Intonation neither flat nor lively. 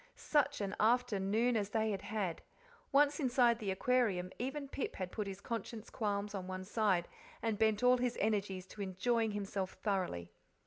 Yes: average, 3.9 semitones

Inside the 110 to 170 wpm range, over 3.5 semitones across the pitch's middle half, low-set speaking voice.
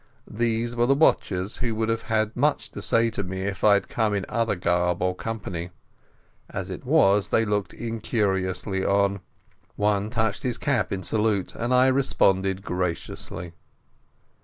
No: average, 160 wpm; average, 3.2 semitones; low, 105 Hz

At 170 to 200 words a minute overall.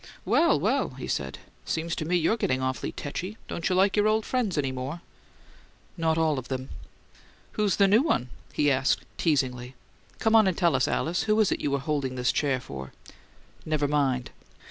Yes: average, 190 wpm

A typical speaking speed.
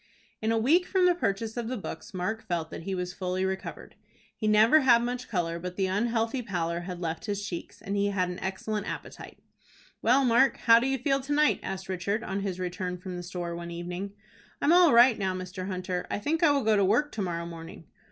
No: fast, 230 wpm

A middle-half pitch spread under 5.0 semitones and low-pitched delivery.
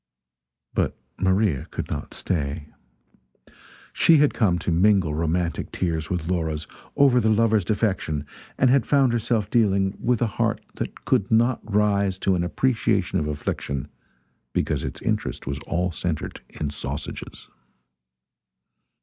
No: wide, 5.4 semitones; very low, 95 Hz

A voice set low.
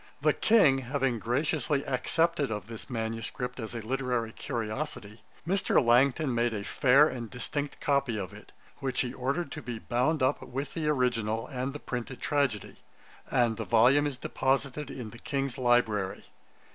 Yes: low, 125 Hz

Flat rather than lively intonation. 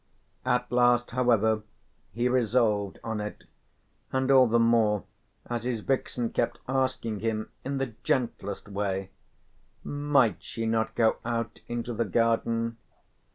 Yes: narrow, 2.0 semitones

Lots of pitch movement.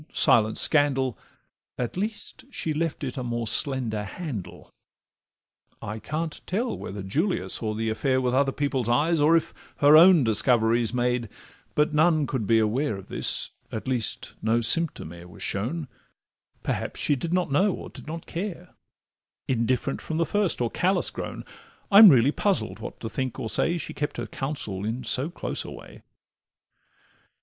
Yes: wide, 6.2 semitones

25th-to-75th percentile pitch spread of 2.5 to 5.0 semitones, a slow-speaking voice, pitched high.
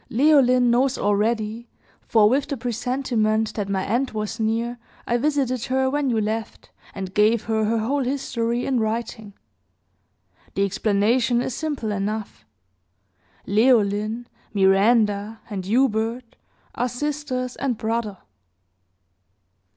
Yes: average, 3.0 semitones; slow, 120 wpm; high, 230 Hz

